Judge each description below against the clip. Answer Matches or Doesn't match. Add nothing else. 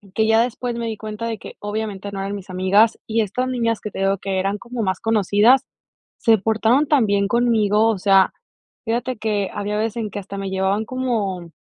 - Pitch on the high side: Matches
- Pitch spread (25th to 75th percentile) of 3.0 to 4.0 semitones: Doesn't match